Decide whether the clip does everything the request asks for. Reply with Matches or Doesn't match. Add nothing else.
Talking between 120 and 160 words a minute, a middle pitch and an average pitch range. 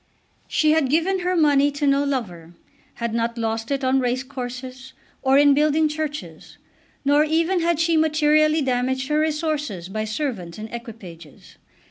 Doesn't match